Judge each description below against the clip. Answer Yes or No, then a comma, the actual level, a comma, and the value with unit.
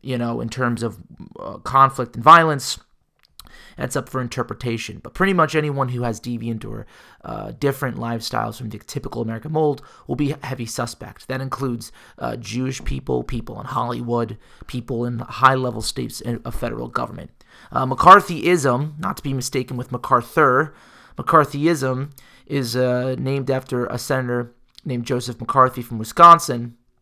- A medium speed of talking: Yes, average, 155 wpm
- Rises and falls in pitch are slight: Yes, narrow, 2.3 semitones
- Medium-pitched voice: No, low, 125 Hz